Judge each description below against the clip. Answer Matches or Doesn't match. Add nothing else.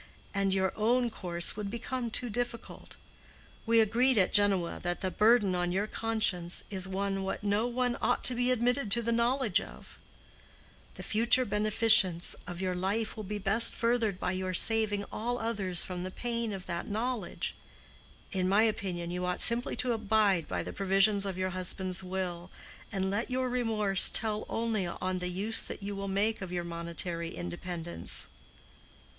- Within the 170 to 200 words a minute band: Matches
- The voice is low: Doesn't match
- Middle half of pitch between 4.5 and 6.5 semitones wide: Doesn't match